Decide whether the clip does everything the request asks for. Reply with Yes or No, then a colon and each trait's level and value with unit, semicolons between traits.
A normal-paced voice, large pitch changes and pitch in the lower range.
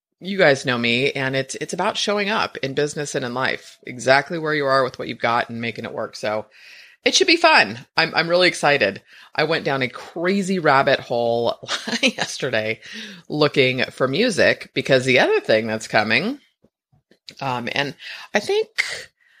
No: average, 175 wpm; wide, 8.7 semitones; medium, 150 Hz